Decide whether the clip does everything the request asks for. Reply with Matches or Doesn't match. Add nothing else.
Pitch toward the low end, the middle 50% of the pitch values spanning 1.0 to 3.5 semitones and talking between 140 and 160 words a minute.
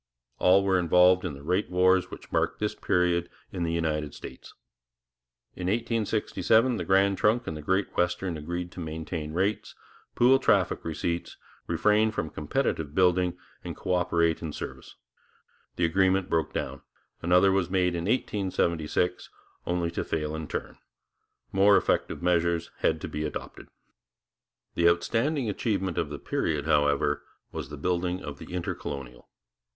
Matches